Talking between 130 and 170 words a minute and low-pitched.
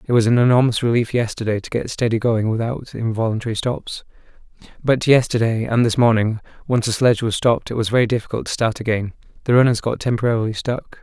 No: average, 185 wpm; low, 115 Hz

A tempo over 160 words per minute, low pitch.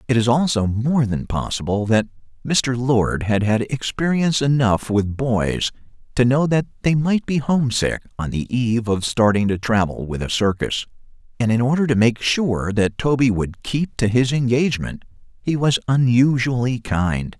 Yes: average, 170 wpm; low, 120 Hz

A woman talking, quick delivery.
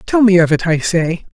No: male; fast, 265 wpm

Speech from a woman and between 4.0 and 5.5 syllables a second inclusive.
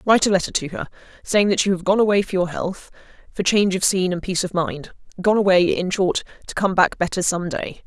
No: female; 6.1 syllables/s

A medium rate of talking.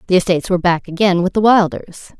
No: fast, 220 wpm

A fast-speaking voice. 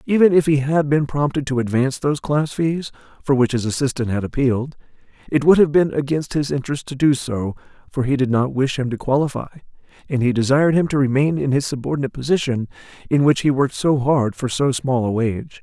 Yes: fast, 215 wpm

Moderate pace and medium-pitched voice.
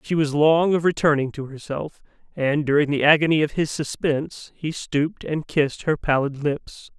Yes: average, 180 wpm; medium, 150 Hz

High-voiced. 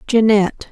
Yes: high, 215 Hz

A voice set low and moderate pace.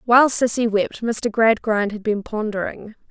No: high, 220 Hz; average, 155 wpm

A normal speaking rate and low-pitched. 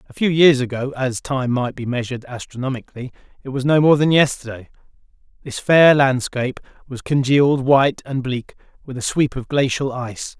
Yes: average, 160 wpm; low, 130 Hz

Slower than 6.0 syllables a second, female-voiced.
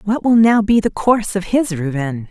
Yes: 5.5 syllables/s; female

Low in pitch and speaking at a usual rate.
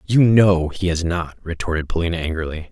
Yes: very low, 85 Hz; average, 175 wpm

